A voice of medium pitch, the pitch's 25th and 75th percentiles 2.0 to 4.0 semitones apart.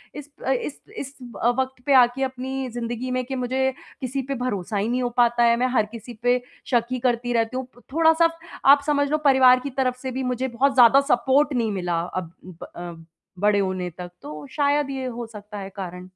No: very high, 250 Hz; average, 2.8 semitones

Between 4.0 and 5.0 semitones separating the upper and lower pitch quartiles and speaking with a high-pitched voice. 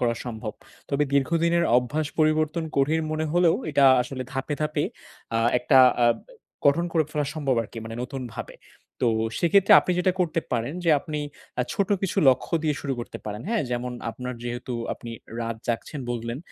No: average, 4.6 semitones; medium, 140 Hz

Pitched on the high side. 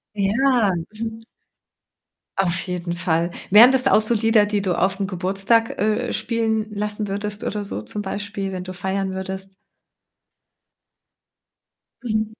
Yes: high, 205 Hz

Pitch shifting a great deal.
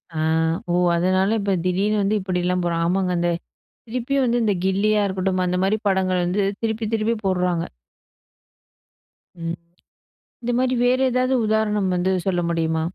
No: average, 3.3 semitones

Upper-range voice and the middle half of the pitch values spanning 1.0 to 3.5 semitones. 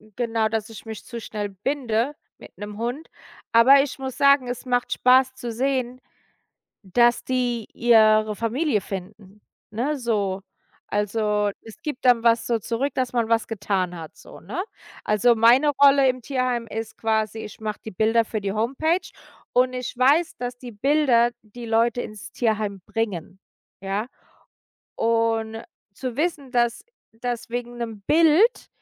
Yes: high, 230 Hz; average, 2.8 semitones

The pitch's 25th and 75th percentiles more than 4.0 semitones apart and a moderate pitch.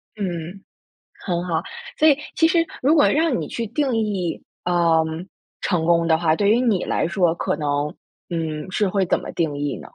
Yes: wide, 5.6 semitones; medium, 180 Hz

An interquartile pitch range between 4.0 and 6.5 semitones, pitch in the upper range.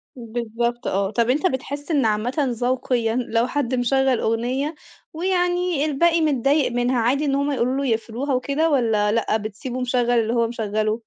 No: average, 3.4 semitones; very high, 250 Hz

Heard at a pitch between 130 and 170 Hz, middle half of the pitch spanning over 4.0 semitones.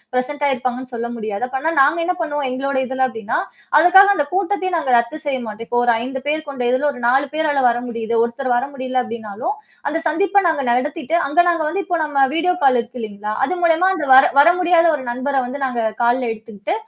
No: very high, 270 Hz; average, 4.7 semitones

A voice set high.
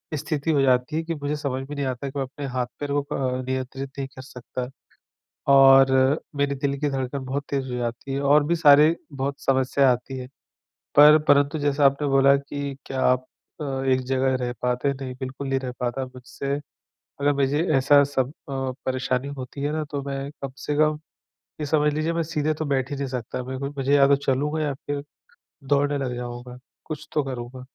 No: low, 135 Hz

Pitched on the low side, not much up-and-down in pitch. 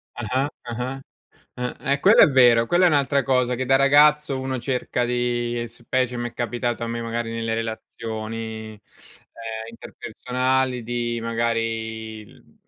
Yes: low, 120 Hz; narrow, 2.2 semitones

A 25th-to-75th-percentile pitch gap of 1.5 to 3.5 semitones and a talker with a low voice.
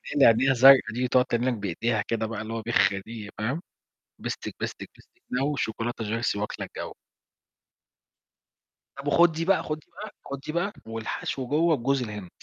No: average, 3.9 semitones; low, 120 Hz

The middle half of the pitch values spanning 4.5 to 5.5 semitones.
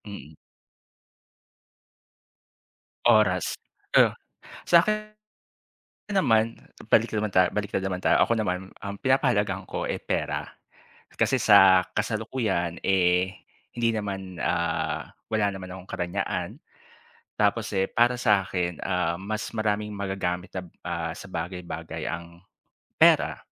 No: average, 3.2 semitones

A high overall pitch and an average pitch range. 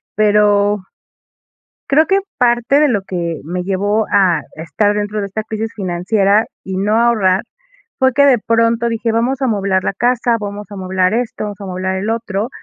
Yes: high, 210 Hz; average, 3.2 semitones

